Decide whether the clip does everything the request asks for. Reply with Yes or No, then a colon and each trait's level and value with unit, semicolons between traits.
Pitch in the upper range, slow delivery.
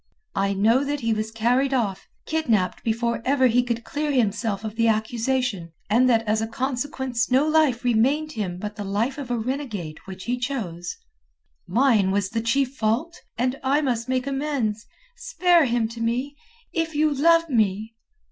No: high, 240 Hz; average, 175 wpm